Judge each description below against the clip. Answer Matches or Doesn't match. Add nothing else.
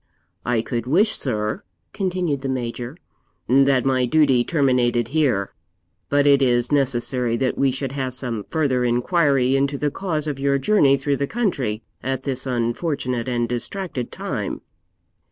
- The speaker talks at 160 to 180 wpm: Doesn't match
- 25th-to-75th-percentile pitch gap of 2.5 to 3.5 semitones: Matches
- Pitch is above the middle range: Doesn't match